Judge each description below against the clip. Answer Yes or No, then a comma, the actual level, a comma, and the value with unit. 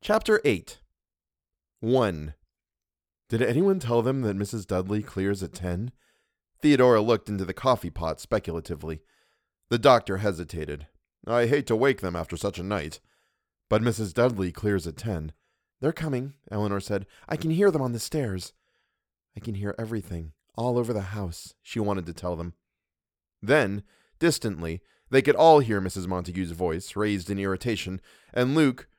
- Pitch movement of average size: No, wide, 5.8 semitones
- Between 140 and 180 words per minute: Yes, average, 155 wpm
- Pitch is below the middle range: Yes, low, 100 Hz